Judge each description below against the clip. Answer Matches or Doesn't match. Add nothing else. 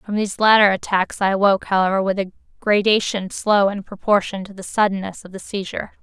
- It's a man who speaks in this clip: Doesn't match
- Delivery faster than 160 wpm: Matches